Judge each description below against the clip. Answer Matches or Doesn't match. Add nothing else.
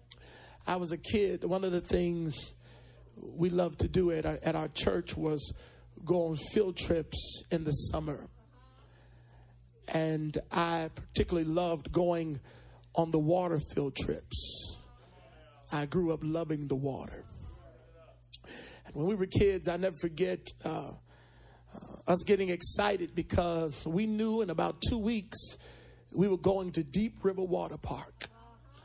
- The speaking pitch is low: Doesn't match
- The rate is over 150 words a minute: Doesn't match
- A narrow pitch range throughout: Doesn't match